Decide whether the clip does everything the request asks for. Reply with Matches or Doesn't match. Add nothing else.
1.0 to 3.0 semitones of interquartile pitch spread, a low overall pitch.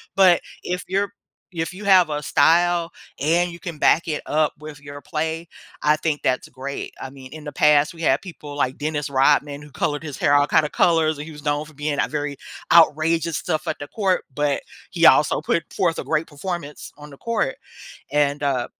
Doesn't match